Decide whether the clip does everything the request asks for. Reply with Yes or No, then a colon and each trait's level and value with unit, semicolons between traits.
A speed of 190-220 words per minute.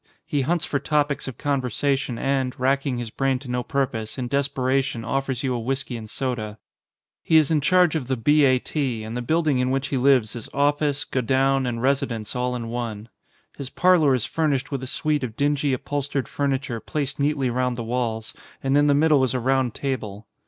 Yes: fast, 205 wpm